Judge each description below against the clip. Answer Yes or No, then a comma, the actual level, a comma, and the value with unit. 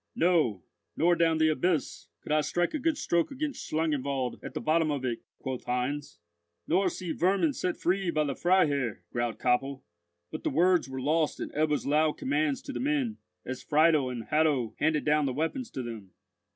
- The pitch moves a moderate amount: Yes, average, 4.6 semitones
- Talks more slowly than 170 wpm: No, average, 190 wpm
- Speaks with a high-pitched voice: No, medium, 155 Hz